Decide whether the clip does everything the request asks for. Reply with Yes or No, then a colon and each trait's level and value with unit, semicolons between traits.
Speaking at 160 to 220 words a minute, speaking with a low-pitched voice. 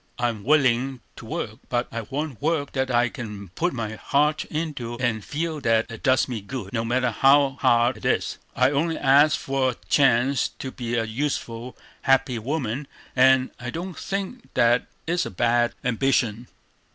Yes: average, 175 wpm; low, 130 Hz